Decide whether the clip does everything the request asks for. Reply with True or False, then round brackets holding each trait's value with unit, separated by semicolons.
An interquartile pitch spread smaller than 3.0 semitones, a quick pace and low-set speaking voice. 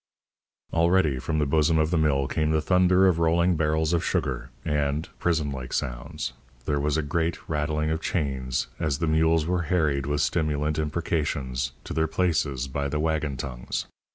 False (2.4 semitones; 175 wpm; 75 Hz)